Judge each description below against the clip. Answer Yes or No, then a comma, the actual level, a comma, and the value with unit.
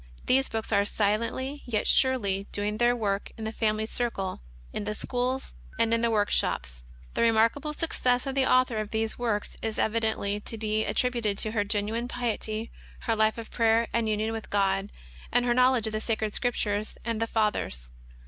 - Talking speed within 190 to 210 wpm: Yes, average, 195 wpm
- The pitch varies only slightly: Yes, narrow, 2.3 semitones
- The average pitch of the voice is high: Yes, high, 220 Hz